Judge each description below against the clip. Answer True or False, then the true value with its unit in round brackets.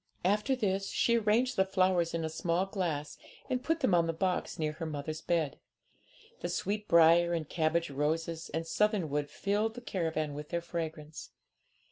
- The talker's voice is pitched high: False (170 Hz)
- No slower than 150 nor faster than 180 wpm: True (170 wpm)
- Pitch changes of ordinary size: True (3.8 semitones)